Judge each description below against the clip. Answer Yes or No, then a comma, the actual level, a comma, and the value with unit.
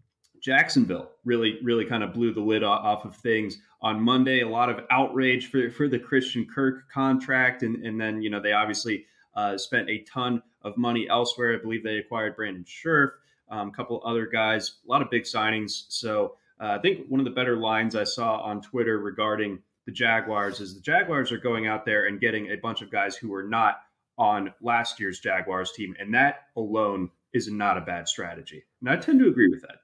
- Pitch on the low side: Yes, low, 115 Hz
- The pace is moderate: No, fast, 210 wpm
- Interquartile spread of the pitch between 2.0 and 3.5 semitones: Yes, narrow, 2.6 semitones